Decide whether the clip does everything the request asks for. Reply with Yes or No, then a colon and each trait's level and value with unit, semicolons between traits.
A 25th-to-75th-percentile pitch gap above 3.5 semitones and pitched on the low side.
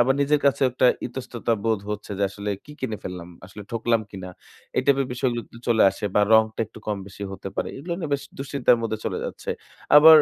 Yes: average, 4.5 semitones; low, 120 Hz